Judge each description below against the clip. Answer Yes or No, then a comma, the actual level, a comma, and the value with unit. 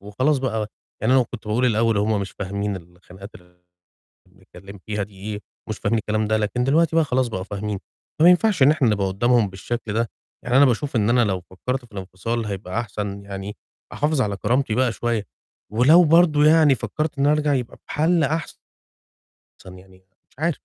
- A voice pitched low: Yes, low, 115 Hz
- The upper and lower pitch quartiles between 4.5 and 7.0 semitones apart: Yes, average, 5.2 semitones